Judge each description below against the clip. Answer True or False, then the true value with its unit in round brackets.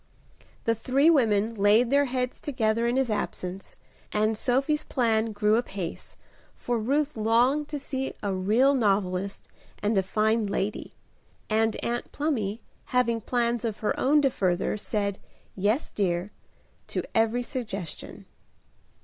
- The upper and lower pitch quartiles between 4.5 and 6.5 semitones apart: False (3.6 semitones)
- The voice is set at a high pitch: True (225 Hz)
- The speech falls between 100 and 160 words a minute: True (135 wpm)